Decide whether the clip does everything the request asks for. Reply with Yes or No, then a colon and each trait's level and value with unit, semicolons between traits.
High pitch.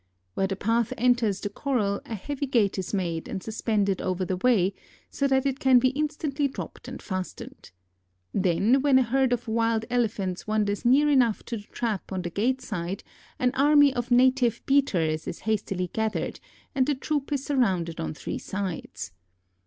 Yes: high, 225 Hz